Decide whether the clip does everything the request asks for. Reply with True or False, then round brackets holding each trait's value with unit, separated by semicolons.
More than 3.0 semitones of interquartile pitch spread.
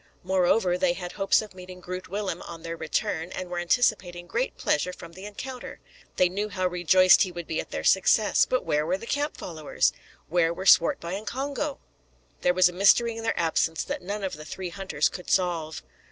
False (2.6 semitones)